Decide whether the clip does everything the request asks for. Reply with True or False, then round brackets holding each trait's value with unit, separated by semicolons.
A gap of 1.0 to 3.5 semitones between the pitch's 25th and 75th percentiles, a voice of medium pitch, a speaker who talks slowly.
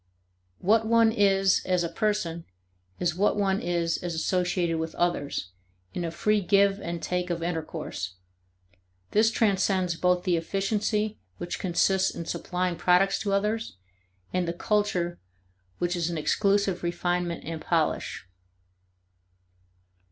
True (2.7 semitones; 180 Hz; 130 wpm)